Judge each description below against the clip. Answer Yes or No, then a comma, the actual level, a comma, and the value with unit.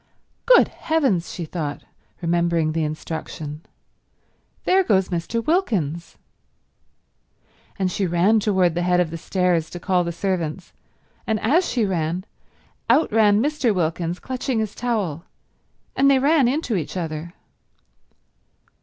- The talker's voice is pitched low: No, medium, 185 Hz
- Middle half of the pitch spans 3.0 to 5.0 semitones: No, wide, 5.5 semitones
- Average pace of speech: No, slow, 130 wpm